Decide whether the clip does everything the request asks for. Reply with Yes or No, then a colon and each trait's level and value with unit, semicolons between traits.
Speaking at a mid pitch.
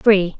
No: high, 195 Hz